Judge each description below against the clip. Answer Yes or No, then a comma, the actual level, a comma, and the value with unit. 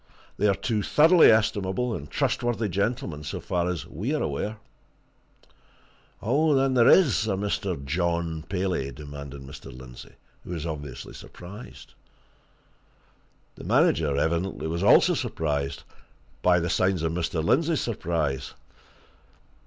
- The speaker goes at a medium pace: No, slow, 125 wpm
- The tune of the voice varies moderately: No, wide, 6.2 semitones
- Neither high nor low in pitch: No, very low, 90 Hz